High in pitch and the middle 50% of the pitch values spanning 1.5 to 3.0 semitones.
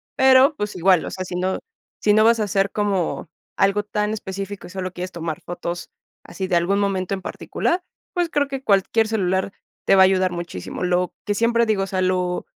Yes: high, 195 Hz; narrow, 2.6 semitones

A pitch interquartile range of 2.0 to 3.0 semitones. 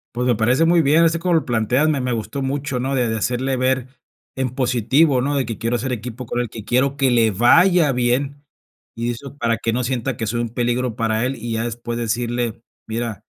Yes: narrow, 2.6 semitones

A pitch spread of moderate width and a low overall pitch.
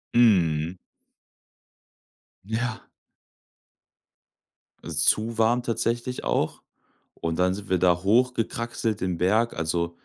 Yes: average, 4.8 semitones; low, 105 Hz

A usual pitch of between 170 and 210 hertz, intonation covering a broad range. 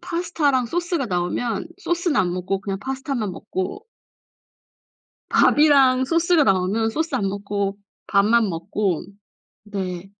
No: high, 225 Hz; wide, 7.1 semitones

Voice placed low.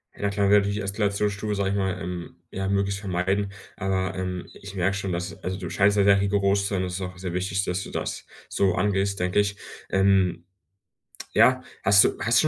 Yes: low, 100 Hz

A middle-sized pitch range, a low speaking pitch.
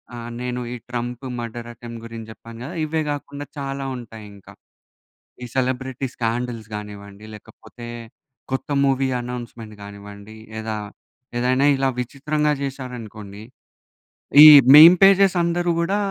Yes: average, 3.7 semitones; low, 125 Hz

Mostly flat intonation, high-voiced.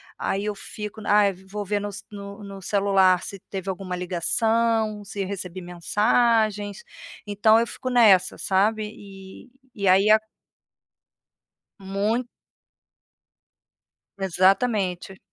Yes: narrow, 2.0 semitones; high, 200 Hz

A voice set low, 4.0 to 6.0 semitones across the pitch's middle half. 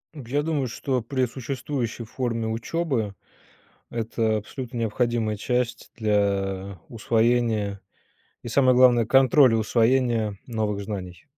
No: low, 115 Hz; average, 3.0 semitones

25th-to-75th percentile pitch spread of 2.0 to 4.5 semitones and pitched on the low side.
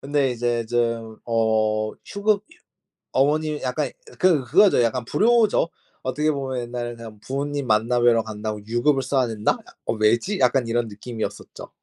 Yes: average, 4.0 semitones; low, 120 Hz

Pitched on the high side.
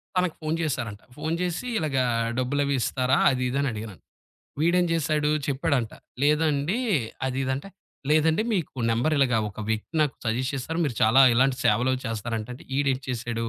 No: low, 135 Hz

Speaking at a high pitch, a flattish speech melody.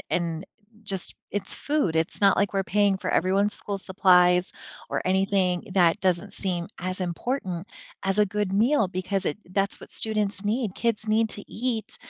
Yes: high, 195 Hz; narrow, 2.3 semitones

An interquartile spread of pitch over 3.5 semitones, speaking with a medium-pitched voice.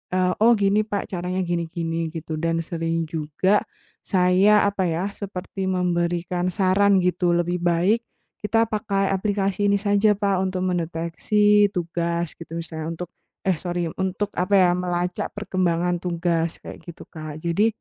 No: average, 2.8 semitones; medium, 180 Hz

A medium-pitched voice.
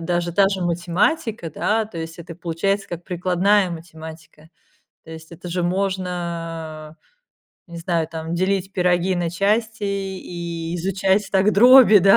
Yes: medium, 175 Hz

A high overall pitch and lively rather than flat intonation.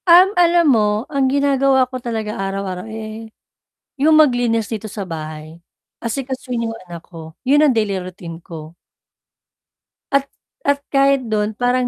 Yes: high, 225 Hz; wide, 5.8 semitones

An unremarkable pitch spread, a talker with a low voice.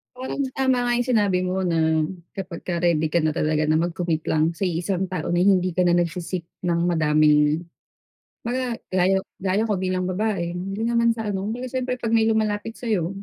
No: average, 4.5 semitones; medium, 185 Hz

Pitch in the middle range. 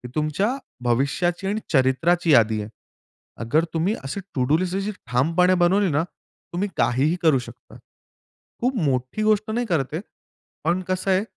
Yes: medium, 165 Hz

